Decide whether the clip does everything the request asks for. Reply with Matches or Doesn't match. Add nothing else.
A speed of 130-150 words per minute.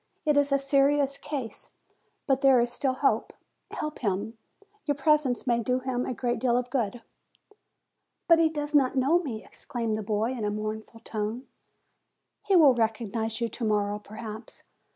Doesn't match